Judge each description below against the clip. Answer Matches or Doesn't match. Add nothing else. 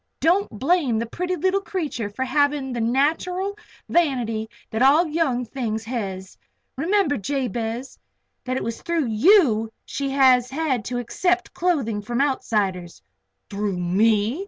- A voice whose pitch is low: Doesn't match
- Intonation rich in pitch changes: Matches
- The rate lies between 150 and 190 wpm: Doesn't match